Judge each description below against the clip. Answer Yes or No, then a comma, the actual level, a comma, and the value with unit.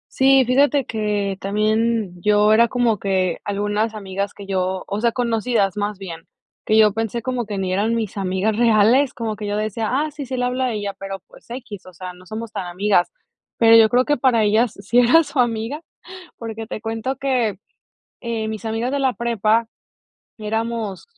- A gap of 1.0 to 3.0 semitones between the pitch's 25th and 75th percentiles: Yes, average, 2.7 semitones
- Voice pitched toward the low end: No, high, 220 Hz